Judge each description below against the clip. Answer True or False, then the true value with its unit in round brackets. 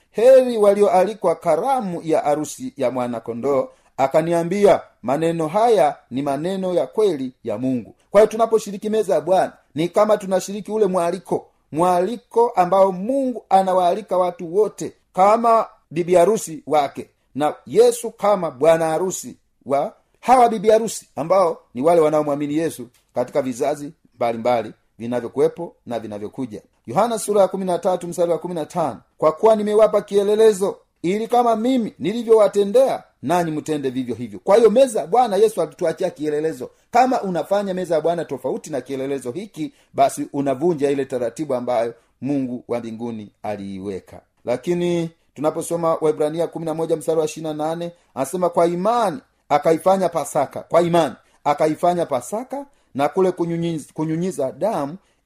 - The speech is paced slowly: False (115 wpm)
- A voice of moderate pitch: True (170 Hz)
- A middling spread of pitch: False (5.9 semitones)